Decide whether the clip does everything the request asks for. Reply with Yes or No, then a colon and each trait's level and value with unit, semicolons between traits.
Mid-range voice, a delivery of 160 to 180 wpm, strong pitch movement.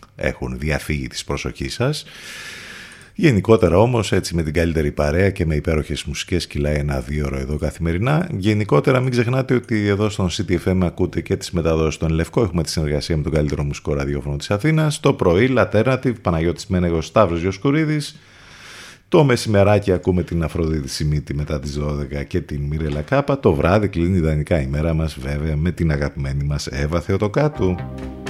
No: very low, 85 Hz; average, 165 wpm; wide, 6.0 semitones